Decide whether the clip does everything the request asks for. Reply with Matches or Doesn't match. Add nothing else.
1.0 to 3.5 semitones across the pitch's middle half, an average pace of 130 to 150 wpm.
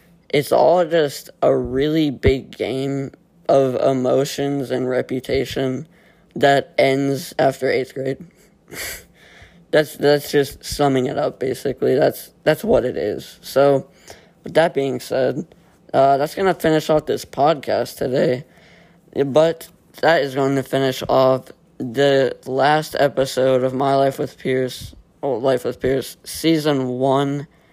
Matches